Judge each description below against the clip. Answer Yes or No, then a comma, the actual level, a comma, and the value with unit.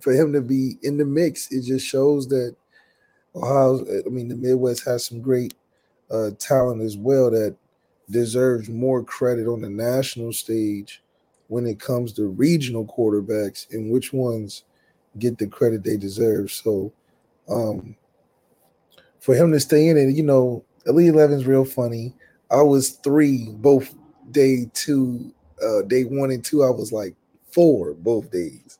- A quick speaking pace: No, average, 160 wpm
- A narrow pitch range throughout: No, average, 3.0 semitones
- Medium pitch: No, low, 125 Hz